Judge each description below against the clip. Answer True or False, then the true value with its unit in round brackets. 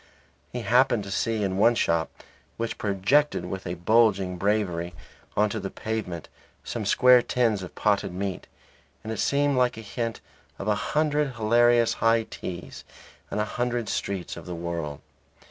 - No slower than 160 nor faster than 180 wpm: True (165 wpm)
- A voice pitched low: True (105 Hz)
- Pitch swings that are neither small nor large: True (4.0 semitones)